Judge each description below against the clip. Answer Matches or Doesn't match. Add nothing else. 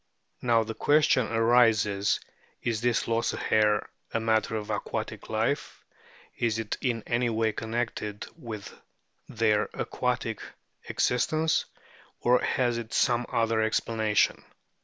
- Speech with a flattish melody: Matches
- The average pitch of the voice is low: Matches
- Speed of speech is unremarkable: Doesn't match